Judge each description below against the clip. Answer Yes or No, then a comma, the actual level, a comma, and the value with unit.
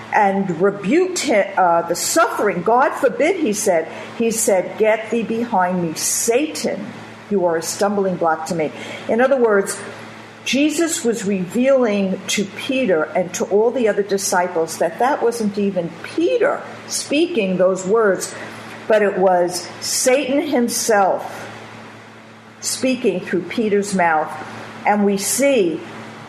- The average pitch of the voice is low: No, high, 200 Hz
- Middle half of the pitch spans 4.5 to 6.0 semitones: Yes, average, 5.1 semitones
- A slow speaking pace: Yes, slow, 130 wpm